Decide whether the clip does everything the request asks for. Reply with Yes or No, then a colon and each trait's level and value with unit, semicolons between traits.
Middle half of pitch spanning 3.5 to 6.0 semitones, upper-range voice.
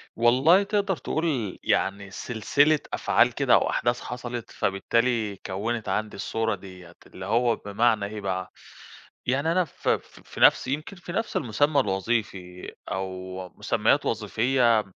No: average, 5.0 semitones; low, 115 Hz